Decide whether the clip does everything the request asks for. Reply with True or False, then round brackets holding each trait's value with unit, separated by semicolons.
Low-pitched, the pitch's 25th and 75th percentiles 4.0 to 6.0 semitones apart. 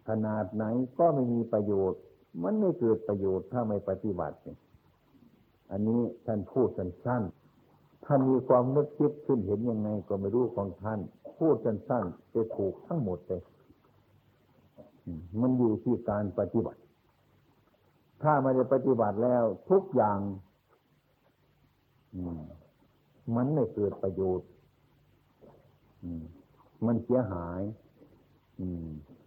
True (110 Hz; 4.7 semitones)